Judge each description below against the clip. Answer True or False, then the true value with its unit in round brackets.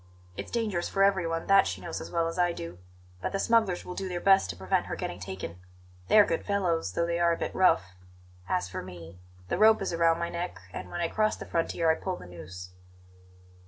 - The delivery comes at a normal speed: False (235 wpm)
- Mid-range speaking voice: True (170 Hz)